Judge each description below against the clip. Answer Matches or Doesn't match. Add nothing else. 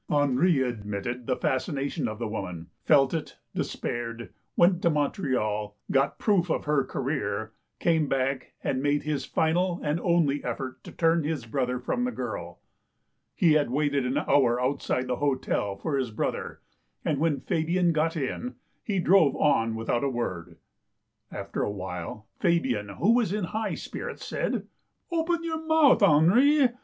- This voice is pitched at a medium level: Matches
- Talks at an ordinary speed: Matches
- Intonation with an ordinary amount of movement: Doesn't match